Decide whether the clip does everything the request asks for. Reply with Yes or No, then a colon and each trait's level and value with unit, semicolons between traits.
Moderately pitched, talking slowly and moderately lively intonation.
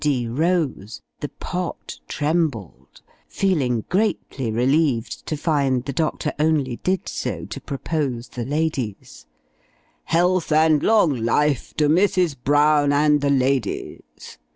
Yes: medium, 145 Hz; slow, 120 wpm; average, 3.9 semitones